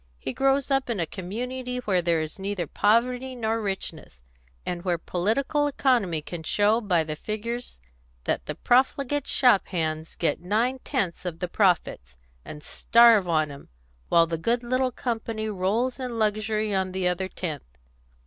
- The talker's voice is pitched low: No, high, 205 Hz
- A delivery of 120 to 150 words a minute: No, average, 160 wpm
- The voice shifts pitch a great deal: Yes, wide, 5.9 semitones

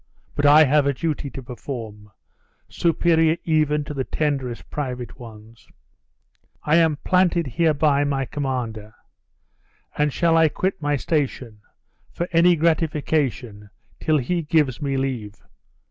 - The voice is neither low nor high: Yes, medium, 145 Hz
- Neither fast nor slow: No, slow, 130 wpm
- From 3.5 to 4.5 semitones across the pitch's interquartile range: Yes, average, 4.0 semitones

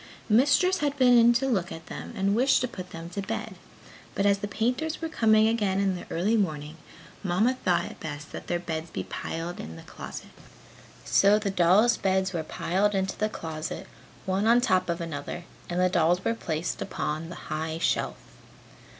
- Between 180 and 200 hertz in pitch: Yes, high, 190 Hz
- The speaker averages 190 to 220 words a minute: Yes, average, 195 wpm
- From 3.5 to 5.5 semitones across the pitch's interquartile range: Yes, average, 4.7 semitones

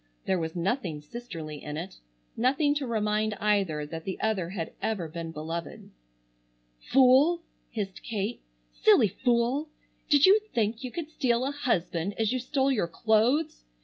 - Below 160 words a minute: Yes, average, 150 wpm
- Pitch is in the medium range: No, high, 215 Hz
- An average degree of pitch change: No, wide, 7.0 semitones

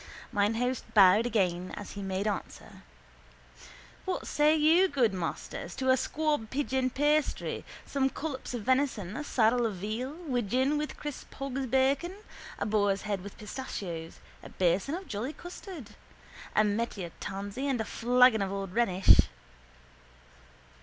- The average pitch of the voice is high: Yes, high, 240 Hz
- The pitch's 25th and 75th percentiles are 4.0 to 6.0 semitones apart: Yes, average, 5.3 semitones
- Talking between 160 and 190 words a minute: No, average, 145 wpm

